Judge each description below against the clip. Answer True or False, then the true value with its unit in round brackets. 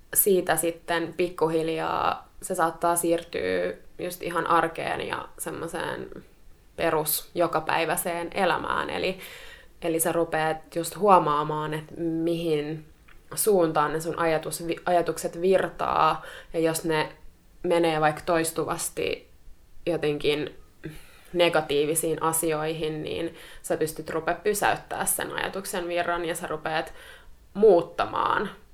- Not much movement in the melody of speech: True (1.7 semitones)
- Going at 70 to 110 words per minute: True (100 wpm)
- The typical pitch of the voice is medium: True (165 Hz)